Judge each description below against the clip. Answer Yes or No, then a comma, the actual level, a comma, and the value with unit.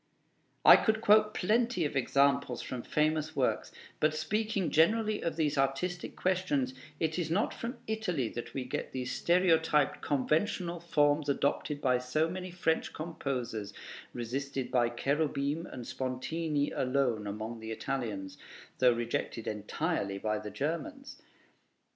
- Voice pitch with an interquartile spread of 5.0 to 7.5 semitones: Yes, average, 5.3 semitones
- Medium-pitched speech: Yes, medium, 145 Hz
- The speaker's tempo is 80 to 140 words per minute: Yes, slow, 135 wpm